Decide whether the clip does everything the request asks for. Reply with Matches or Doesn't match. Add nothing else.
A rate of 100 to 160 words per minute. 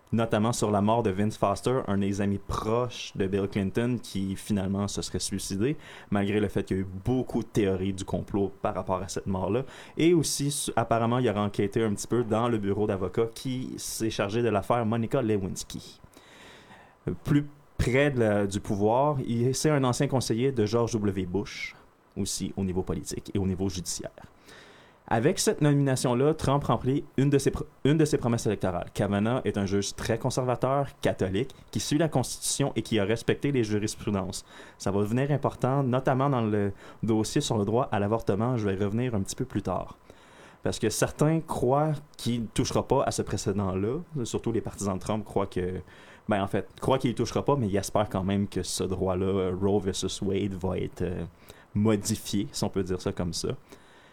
Doesn't match